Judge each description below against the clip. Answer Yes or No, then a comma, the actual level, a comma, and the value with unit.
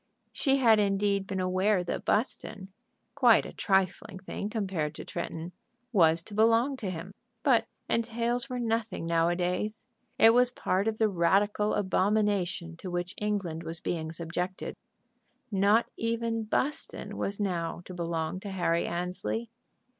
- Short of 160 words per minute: Yes, average, 140 wpm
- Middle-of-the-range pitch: No, high, 195 Hz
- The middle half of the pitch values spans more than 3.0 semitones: Yes, average, 4.1 semitones